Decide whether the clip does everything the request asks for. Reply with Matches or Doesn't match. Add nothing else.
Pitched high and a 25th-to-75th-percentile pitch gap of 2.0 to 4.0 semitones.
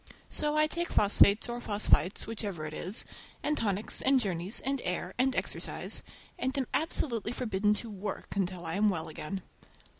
Doesn't match